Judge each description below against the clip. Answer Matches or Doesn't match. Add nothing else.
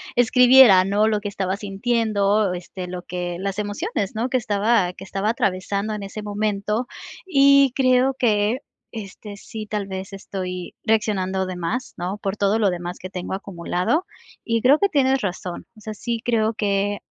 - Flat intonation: Doesn't match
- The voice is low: Doesn't match